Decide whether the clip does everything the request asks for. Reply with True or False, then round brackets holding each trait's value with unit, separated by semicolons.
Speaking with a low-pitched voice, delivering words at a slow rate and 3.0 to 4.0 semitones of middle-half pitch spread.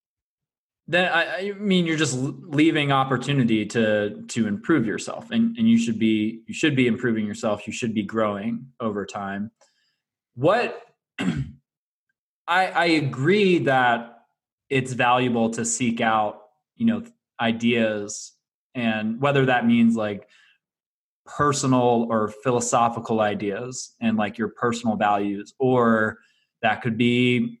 True (115 Hz; 125 wpm; 3.5 semitones)